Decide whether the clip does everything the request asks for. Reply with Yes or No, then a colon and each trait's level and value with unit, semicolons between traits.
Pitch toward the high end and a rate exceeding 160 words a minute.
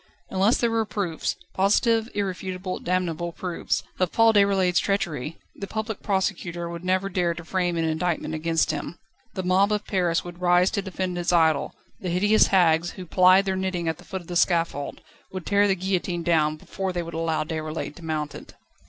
No: medium, 180 Hz; average, 190 wpm